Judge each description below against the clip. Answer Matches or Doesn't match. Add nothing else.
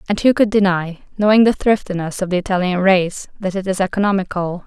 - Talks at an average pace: Matches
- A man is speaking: Doesn't match